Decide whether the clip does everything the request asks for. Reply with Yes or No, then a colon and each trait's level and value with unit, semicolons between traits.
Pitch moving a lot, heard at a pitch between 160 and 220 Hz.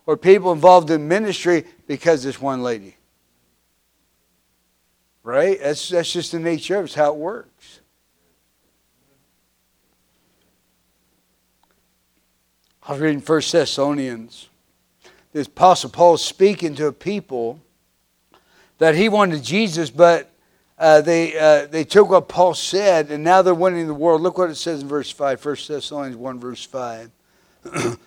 No: wide, 6.4 semitones; medium, 150 Hz